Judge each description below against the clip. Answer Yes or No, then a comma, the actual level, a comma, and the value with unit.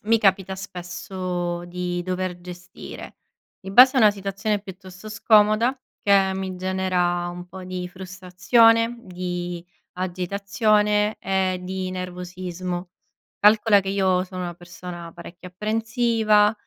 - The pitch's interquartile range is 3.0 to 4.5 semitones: No, narrow, 2.6 semitones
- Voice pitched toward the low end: No, medium, 185 Hz